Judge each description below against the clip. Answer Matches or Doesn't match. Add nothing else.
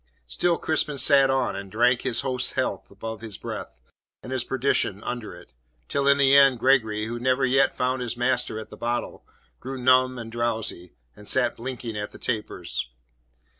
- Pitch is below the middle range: Matches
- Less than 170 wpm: Doesn't match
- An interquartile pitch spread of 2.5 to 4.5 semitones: Matches